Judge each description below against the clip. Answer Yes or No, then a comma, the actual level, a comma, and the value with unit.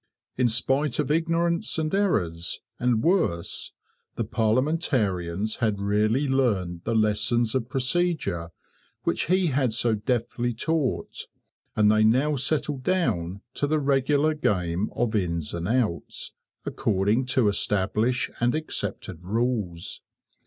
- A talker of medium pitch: No, low, 120 Hz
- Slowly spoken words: Yes, slow, 125 wpm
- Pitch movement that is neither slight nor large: No, wide, 5.9 semitones